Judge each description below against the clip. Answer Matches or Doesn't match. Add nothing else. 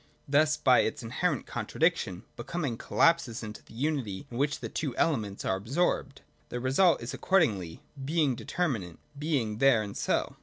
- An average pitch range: Doesn't match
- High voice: Doesn't match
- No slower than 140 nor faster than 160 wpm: Matches